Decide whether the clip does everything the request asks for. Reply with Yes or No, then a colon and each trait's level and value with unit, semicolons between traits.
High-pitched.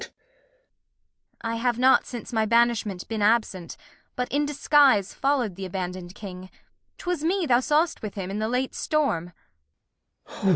Yes: high, 230 Hz